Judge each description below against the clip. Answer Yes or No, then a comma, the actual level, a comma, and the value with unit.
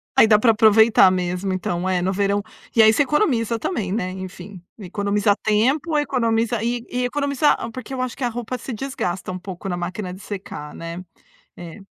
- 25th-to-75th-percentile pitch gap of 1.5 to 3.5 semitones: No, average, 4.8 semitones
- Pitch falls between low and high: No, high, 215 Hz